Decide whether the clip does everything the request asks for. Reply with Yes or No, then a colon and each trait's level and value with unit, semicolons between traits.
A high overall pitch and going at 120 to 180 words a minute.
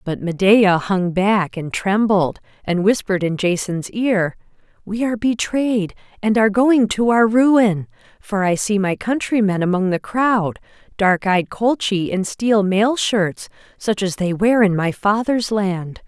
Yes: high, 205 Hz; average, 160 wpm